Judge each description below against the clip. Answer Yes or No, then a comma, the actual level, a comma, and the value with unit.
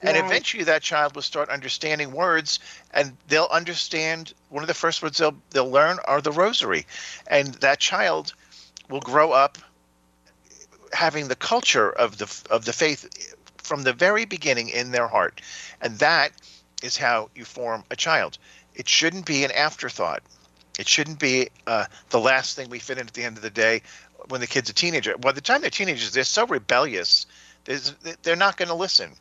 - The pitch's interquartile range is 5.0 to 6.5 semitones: Yes, wide, 5.4 semitones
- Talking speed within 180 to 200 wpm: Yes, average, 185 wpm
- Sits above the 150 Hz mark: No, medium, 145 Hz